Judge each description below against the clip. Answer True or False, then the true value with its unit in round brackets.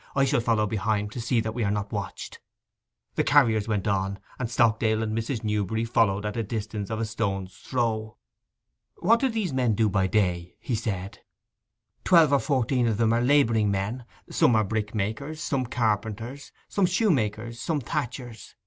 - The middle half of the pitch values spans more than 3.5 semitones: False (3.0 semitones)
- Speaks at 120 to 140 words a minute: False (175 wpm)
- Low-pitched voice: True (110 Hz)